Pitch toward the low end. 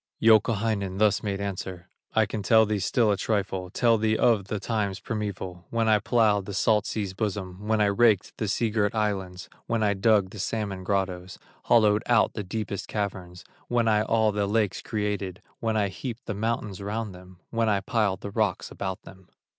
Yes: low, 105 Hz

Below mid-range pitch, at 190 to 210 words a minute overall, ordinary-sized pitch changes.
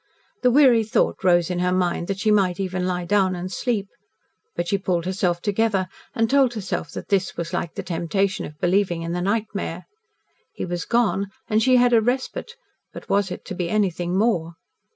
No: high, 190 Hz; average, 195 wpm; average, 3.5 semitones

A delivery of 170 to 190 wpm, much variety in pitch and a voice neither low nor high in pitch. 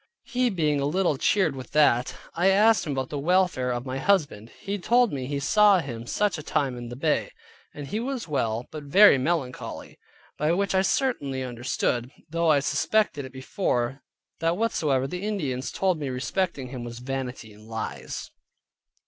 Yes: average, 180 wpm; wide, 6.6 semitones; medium, 145 Hz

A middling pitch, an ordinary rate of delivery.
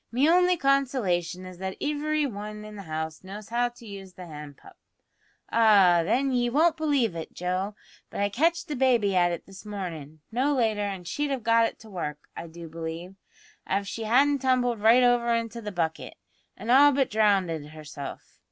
No: high, 210 Hz; average, 190 wpm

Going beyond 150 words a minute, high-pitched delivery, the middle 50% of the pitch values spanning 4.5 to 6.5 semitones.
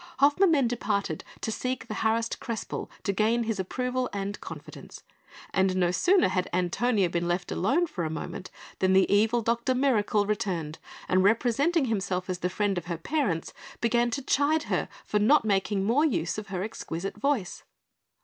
Yes: average, 175 wpm; high, 210 Hz; average, 4.8 semitones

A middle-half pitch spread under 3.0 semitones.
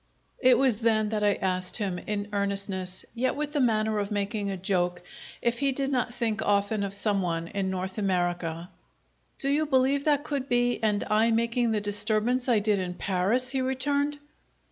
No: average, 4.2 semitones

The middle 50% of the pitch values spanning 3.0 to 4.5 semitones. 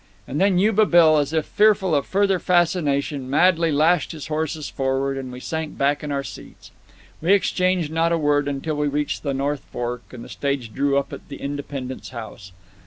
Yes: average, 3.4 semitones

